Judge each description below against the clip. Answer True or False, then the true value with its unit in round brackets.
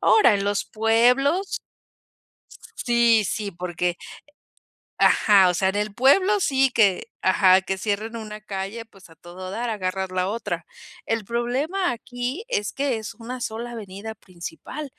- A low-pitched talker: False (220 Hz)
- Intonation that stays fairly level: False (4.2 semitones)